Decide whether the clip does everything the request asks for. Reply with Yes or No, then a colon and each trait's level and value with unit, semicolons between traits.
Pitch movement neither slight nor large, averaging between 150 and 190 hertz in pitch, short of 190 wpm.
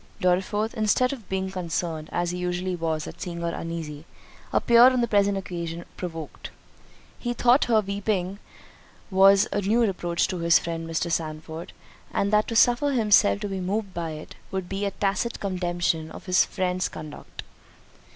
Yes: average, 3.5 semitones; medium, 185 Hz; average, 170 wpm